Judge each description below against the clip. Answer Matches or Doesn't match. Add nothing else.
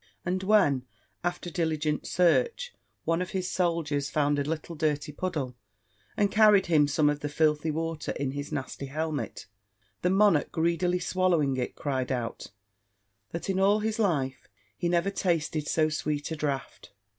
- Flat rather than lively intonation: Doesn't match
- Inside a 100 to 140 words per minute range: Doesn't match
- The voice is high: Doesn't match